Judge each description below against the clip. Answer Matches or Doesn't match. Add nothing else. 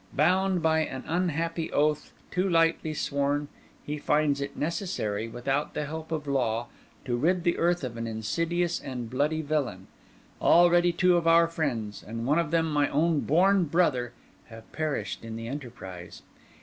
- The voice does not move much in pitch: Doesn't match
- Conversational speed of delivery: Matches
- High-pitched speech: Doesn't match